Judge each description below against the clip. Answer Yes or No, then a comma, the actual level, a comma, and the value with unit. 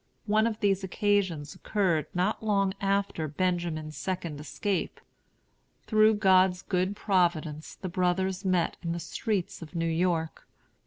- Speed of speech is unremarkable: No, slow, 130 wpm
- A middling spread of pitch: Yes, average, 3.0 semitones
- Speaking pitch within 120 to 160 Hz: No, medium, 185 Hz